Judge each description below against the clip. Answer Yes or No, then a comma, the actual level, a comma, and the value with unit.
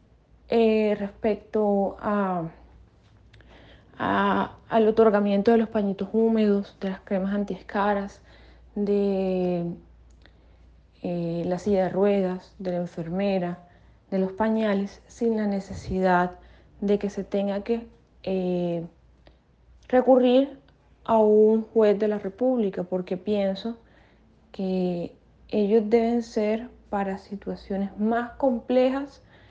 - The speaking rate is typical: No, slow, 105 wpm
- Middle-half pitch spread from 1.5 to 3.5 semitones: Yes, average, 3.0 semitones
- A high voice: Yes, high, 200 Hz